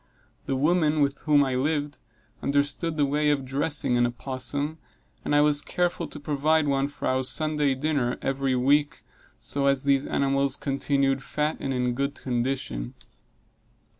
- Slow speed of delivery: No, average, 160 wpm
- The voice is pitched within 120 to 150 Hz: Yes, medium, 140 Hz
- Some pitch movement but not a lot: No, narrow, 1.8 semitones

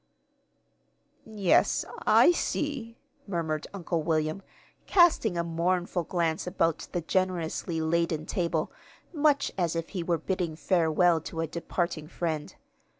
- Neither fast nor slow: No, slow, 120 wpm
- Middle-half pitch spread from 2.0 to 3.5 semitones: Yes, narrow, 2.4 semitones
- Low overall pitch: No, medium, 170 Hz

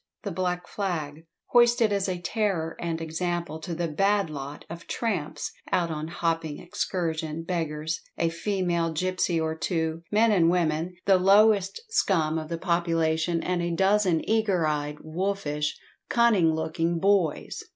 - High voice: No, medium, 170 Hz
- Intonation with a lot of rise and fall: No, average, 3.1 semitones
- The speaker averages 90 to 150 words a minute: Yes, average, 145 wpm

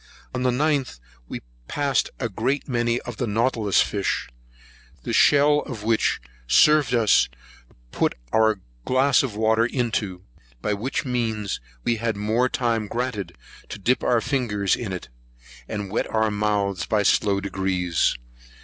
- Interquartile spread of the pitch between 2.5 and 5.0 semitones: Yes, average, 3.6 semitones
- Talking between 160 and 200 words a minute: No, average, 150 wpm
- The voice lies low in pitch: Yes, low, 110 Hz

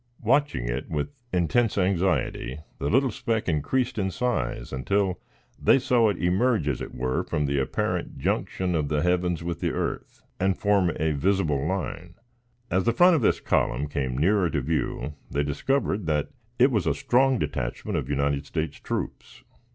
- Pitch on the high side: No, very low, 90 Hz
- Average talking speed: Yes, average, 170 wpm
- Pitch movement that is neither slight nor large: No, wide, 6.6 semitones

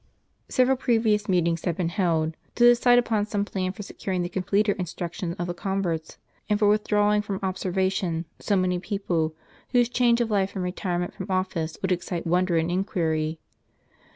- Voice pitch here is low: No, medium, 185 Hz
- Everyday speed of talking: Yes, average, 175 wpm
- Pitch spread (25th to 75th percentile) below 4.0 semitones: Yes, average, 3.1 semitones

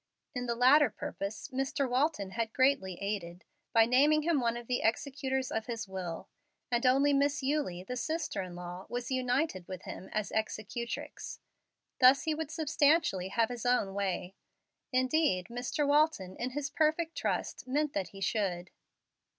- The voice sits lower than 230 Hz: No, high, 245 Hz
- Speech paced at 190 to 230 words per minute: No, average, 160 wpm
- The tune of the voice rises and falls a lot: Yes, wide, 6.3 semitones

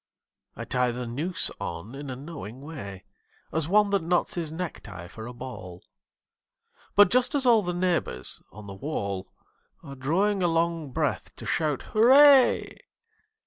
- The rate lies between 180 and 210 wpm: No, average, 155 wpm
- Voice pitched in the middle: Yes, medium, 155 Hz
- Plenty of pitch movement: Yes, wide, 7.1 semitones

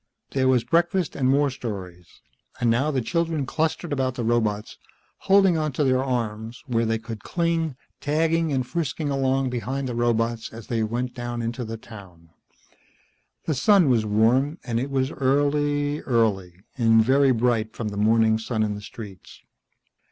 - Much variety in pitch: No, average, 4.2 semitones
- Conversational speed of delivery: Yes, average, 165 wpm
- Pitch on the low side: Yes, low, 125 Hz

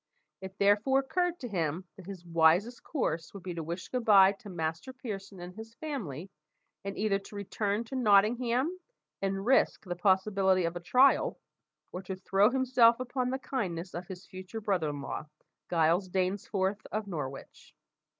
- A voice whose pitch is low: No, high, 195 Hz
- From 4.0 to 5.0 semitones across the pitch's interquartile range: Yes, average, 4.6 semitones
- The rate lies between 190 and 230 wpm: No, average, 170 wpm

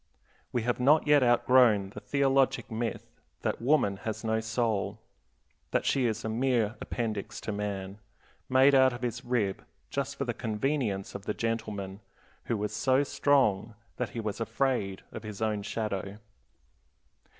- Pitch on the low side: Yes, low, 115 Hz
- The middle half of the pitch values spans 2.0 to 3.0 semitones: No, average, 3.8 semitones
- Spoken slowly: No, average, 155 wpm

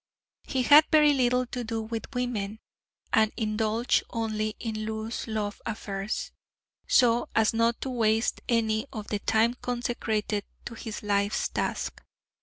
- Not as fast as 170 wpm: Yes, average, 140 wpm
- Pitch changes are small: Yes, narrow, 2.0 semitones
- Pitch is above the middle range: Yes, high, 225 Hz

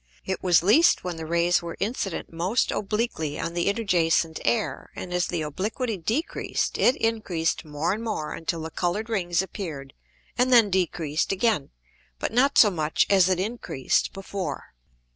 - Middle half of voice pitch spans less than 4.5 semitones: No, average, 4.8 semitones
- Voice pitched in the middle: Yes, medium, 180 Hz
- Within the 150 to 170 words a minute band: Yes, average, 160 wpm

